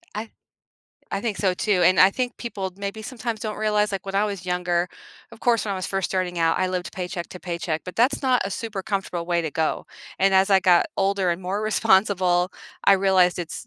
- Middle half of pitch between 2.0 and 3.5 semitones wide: Yes, average, 2.7 semitones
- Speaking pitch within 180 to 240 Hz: Yes, high, 190 Hz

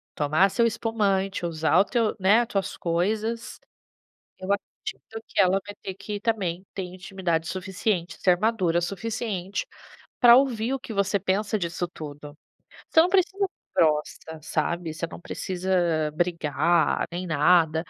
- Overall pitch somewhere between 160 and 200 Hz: Yes, medium, 185 Hz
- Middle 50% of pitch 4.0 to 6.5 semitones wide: Yes, average, 4.3 semitones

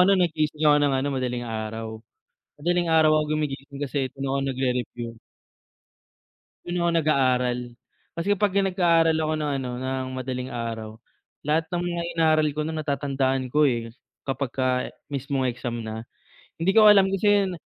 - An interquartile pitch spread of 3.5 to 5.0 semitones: Yes, average, 4.1 semitones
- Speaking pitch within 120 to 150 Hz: Yes, medium, 140 Hz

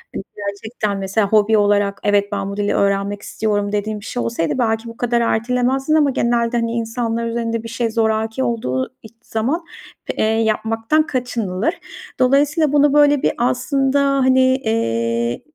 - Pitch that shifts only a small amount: No, average, 3.4 semitones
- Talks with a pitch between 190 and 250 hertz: Yes, high, 225 Hz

